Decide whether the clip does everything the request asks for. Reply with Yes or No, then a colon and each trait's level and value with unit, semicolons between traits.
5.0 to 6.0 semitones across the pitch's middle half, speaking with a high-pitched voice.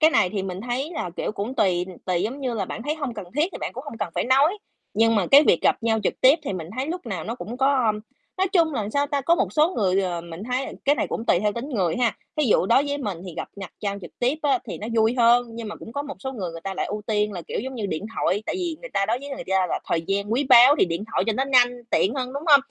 Yes: wide, 5.6 semitones; high, 235 Hz